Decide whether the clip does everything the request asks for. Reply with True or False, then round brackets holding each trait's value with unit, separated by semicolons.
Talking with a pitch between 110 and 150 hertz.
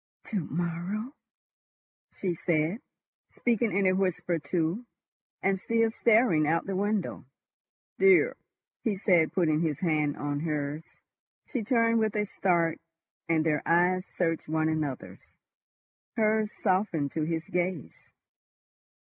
False (175 Hz)